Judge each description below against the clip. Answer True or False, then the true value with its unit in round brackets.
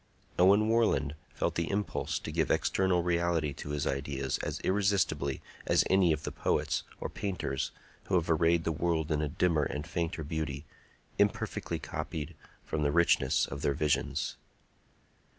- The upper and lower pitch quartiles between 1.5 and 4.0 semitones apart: True (3.3 semitones)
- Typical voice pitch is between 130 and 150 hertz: False (80 Hz)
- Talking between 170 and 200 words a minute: False (155 wpm)